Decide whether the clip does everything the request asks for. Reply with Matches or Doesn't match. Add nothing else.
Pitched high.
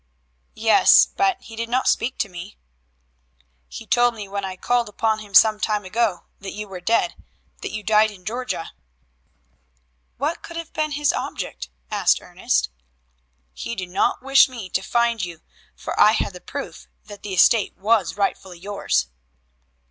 Matches